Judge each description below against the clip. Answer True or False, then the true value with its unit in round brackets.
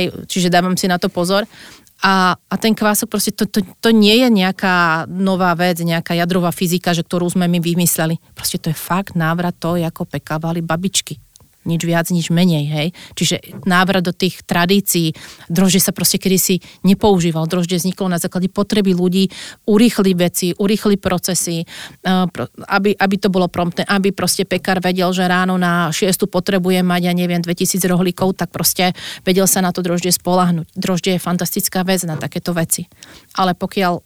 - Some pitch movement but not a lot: False (1.8 semitones)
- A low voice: False (180 Hz)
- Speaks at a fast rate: True (175 wpm)